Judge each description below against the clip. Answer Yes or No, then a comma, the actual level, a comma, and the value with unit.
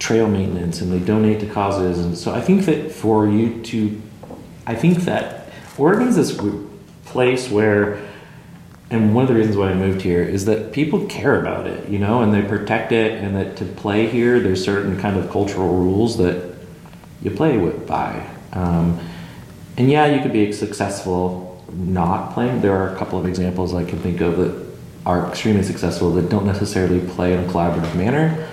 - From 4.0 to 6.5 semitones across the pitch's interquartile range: No, average, 3.4 semitones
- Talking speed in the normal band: Yes, average, 190 wpm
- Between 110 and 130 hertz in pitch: No, low, 100 Hz